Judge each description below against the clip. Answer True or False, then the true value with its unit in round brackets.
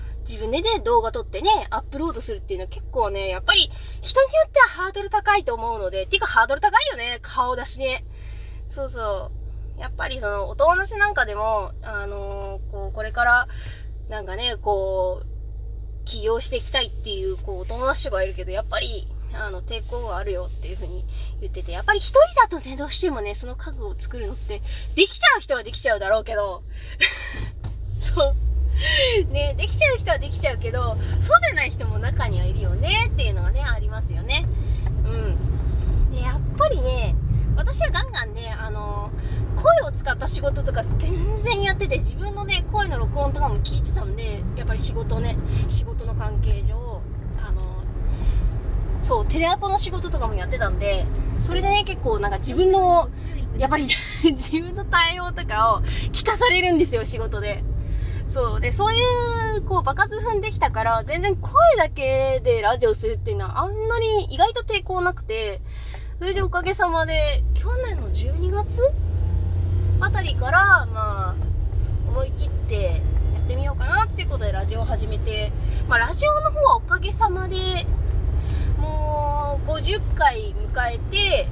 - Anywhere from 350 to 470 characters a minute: False (340 characters per minute)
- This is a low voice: True (115 Hz)